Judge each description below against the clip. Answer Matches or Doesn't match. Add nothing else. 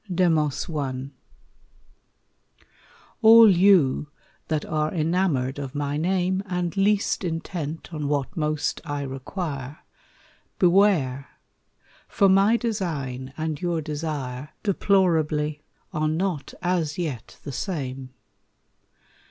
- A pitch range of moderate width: Matches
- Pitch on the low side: Doesn't match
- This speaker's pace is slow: Matches